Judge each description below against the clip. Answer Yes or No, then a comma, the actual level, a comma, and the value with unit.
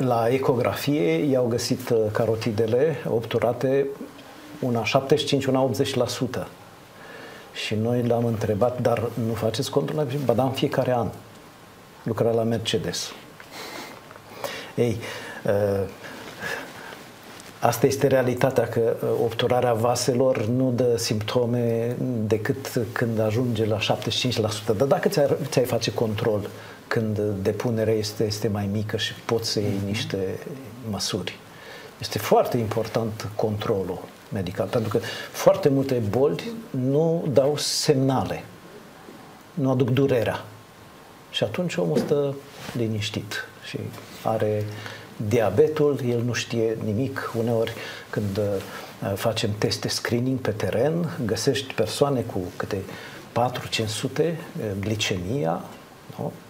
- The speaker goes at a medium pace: No, slow, 105 wpm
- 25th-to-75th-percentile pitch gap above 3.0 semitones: Yes, average, 3.5 semitones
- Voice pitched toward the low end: Yes, low, 120 Hz